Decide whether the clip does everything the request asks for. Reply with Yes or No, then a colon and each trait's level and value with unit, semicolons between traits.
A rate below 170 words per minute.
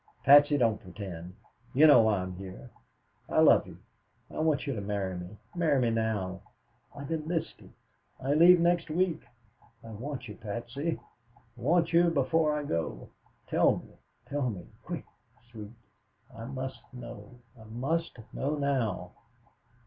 Yes: average, 145 wpm